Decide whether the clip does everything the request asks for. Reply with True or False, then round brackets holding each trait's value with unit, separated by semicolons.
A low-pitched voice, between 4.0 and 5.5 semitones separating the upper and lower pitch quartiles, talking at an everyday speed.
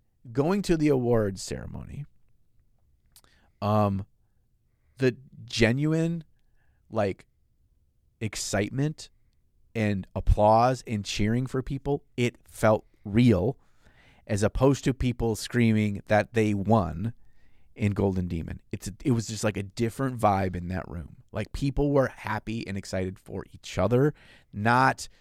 False (110 Hz; 4.7 semitones; 120 wpm)